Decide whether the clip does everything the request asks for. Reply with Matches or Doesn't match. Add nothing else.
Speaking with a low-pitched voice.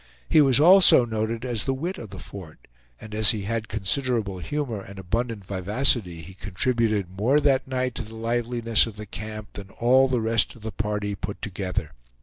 Matches